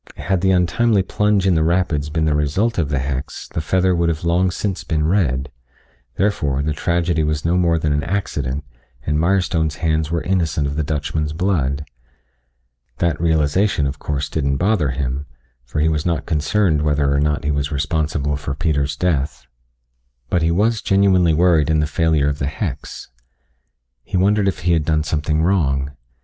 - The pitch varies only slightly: No, average, 3.5 semitones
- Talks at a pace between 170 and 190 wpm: Yes, average, 180 wpm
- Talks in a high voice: No, very low, 80 Hz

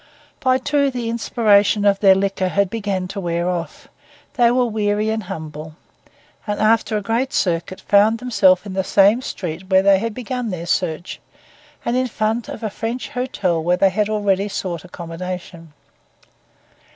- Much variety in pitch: No, average, 3.7 semitones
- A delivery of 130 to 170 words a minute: Yes, average, 165 wpm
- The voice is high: Yes, high, 200 Hz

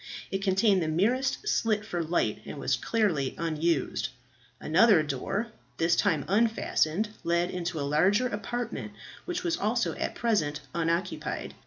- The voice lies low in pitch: No, high, 190 Hz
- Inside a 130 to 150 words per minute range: Yes, average, 140 wpm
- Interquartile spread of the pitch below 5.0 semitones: No, wide, 5.5 semitones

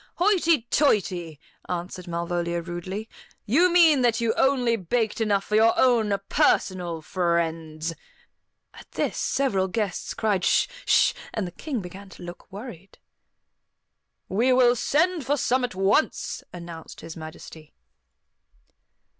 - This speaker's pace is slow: Yes, slow, 130 wpm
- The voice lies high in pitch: Yes, high, 200 Hz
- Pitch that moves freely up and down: Yes, wide, 6.2 semitones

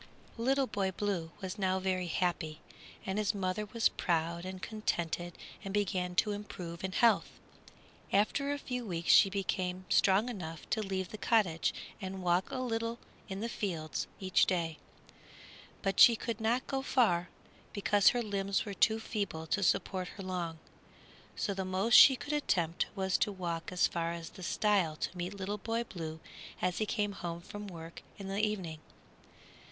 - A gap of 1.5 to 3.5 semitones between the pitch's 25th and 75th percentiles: Yes, average, 3.2 semitones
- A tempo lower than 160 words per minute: No, average, 170 wpm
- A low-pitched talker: No, high, 190 Hz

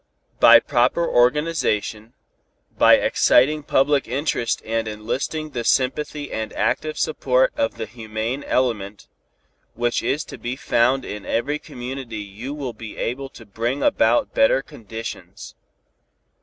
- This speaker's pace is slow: Yes, slow, 130 wpm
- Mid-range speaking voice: No, low, 125 Hz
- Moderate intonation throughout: Yes, average, 4.0 semitones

